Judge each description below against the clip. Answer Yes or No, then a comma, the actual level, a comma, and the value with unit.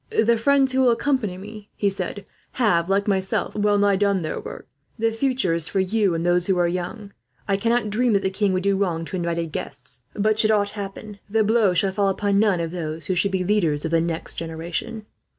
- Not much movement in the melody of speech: No, average, 3.4 semitones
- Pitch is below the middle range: No, high, 200 Hz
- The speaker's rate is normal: No, fast, 230 wpm